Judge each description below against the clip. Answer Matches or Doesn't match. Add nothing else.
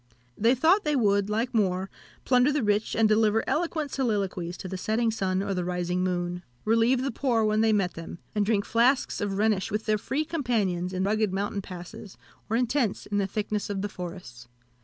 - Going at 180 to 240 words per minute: Matches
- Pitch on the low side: Doesn't match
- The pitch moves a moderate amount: Matches